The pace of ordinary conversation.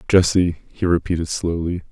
No: slow, 125 wpm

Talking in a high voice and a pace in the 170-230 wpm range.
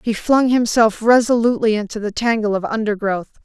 No: high, 220 Hz; average, 155 wpm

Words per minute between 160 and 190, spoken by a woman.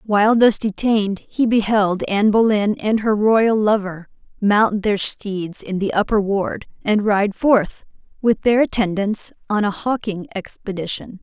No: average, 150 wpm; female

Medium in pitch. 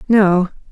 No: high, 195 Hz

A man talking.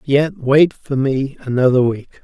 Yes: male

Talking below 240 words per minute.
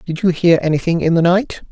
No: fast, 245 wpm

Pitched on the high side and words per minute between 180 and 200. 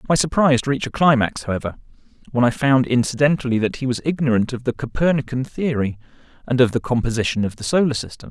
No: low, 130 Hz; average, 190 wpm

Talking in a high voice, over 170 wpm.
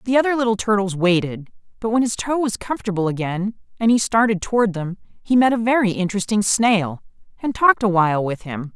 Yes: high, 205 Hz; average, 200 wpm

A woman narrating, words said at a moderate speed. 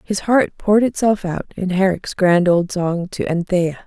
Yes: female; average, 185 wpm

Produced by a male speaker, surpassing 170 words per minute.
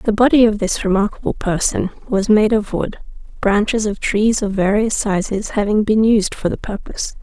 No: female; average, 185 wpm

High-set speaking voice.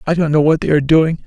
No: medium, 155 Hz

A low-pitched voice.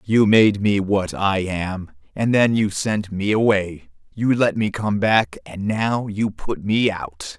Yes: low, 100 Hz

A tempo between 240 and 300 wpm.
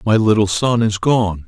No: fast, 205 wpm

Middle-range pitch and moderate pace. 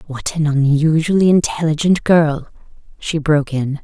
No: medium, 155 Hz; slow, 125 wpm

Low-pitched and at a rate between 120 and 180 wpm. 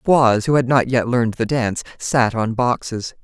No: low, 120 Hz; fast, 205 wpm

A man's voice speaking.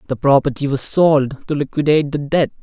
Yes: male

